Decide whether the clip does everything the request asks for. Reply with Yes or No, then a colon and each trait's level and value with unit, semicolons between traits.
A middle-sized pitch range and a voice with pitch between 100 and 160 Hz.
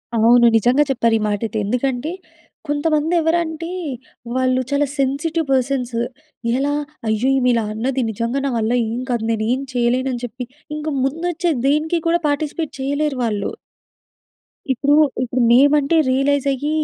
No: average, 3.6 semitones; very high, 265 Hz